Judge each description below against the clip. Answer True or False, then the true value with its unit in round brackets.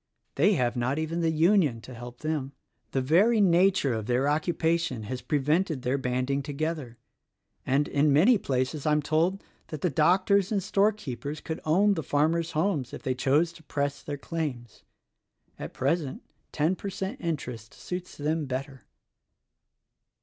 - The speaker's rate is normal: True (165 wpm)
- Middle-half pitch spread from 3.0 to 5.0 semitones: True (4.3 semitones)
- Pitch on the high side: False (150 Hz)